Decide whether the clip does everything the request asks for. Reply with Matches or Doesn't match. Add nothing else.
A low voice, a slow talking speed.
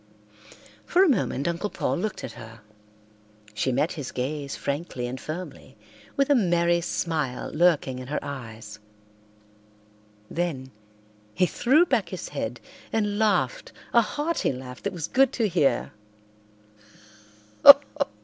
Doesn't match